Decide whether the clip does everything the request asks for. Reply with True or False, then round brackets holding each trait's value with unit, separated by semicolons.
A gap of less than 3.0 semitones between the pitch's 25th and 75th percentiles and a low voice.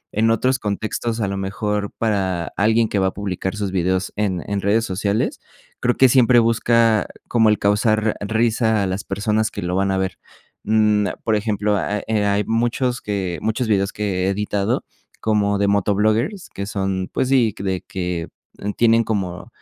True (2.4 semitones; 105 Hz)